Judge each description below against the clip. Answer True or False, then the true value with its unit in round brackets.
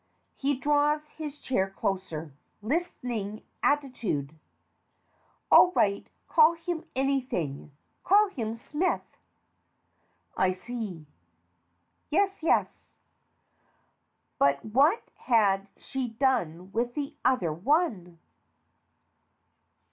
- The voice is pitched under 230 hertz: False (245 Hz)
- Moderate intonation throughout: False (7.6 semitones)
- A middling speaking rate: False (85 wpm)